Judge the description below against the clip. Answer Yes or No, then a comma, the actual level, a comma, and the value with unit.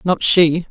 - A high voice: No, medium, 170 Hz